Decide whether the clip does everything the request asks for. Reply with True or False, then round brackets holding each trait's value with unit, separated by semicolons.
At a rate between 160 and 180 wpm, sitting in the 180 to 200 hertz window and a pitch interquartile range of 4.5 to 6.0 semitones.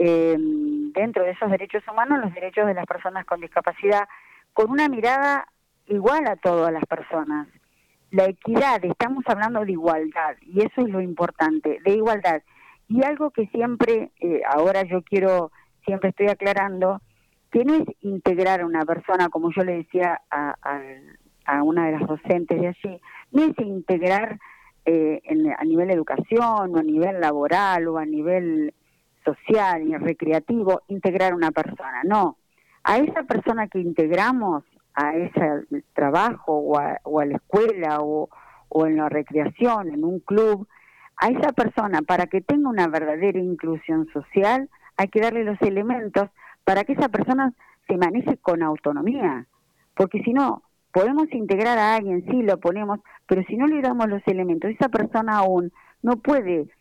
True (165 wpm; 190 Hz; 5.3 semitones)